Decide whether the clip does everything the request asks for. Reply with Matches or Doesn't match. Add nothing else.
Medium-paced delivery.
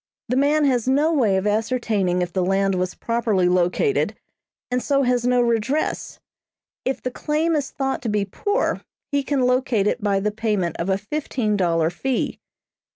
Matches